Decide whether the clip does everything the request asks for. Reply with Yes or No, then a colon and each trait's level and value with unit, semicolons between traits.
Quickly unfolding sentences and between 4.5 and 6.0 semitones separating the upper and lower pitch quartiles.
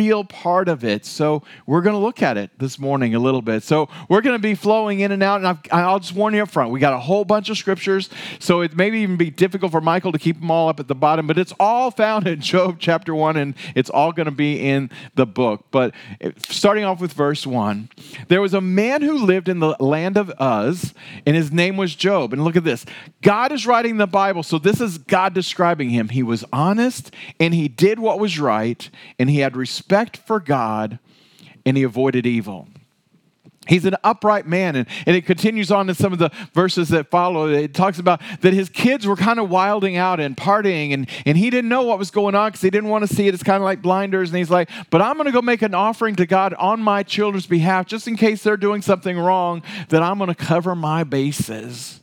Yes: fast, 240 wpm; average, 5.0 semitones